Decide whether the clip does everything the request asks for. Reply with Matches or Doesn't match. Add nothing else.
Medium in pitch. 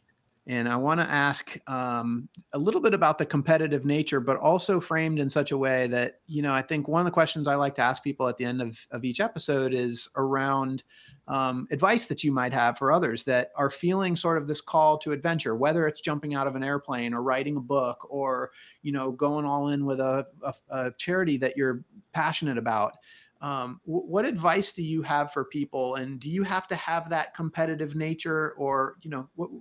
Matches